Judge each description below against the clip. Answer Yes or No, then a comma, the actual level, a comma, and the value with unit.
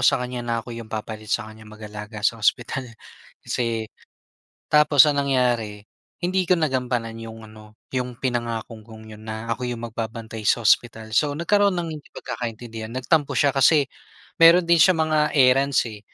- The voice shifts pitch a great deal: No, average, 4.2 semitones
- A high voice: No, low, 120 Hz